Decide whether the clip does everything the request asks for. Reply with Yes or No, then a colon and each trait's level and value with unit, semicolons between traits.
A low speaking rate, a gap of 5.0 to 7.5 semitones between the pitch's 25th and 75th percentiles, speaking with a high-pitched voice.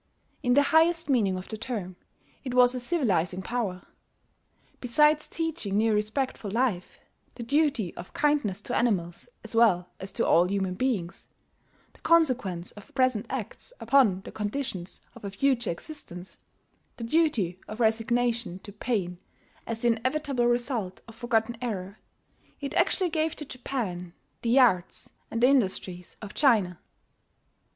No: average, 145 wpm; wide, 5.5 semitones; high, 230 Hz